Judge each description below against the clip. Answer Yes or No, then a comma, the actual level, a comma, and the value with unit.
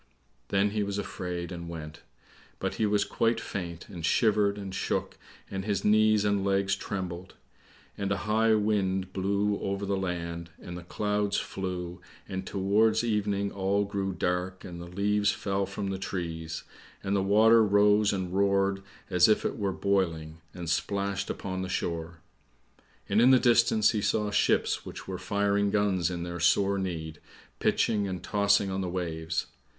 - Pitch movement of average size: No, narrow, 2.3 semitones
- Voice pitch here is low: Yes, low, 100 Hz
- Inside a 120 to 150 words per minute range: No, average, 165 wpm